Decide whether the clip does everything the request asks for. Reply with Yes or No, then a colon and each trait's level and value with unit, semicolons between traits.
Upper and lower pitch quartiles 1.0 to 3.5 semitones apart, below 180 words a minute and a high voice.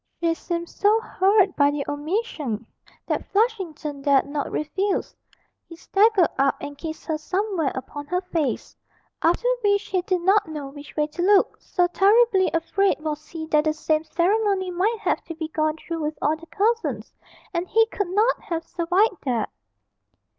No: average, 4.5 semitones; average, 170 wpm; very high, 340 Hz